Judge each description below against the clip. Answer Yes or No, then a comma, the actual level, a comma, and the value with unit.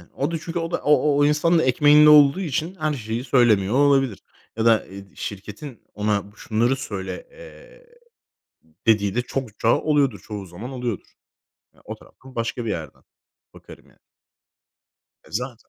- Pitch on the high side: No, low, 130 Hz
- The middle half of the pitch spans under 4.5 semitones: No, wide, 5.6 semitones